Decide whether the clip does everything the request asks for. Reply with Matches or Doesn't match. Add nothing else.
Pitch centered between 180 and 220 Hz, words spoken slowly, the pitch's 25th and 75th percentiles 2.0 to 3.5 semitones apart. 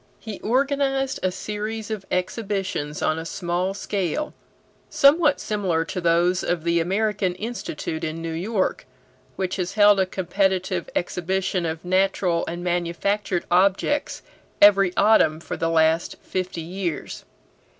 Matches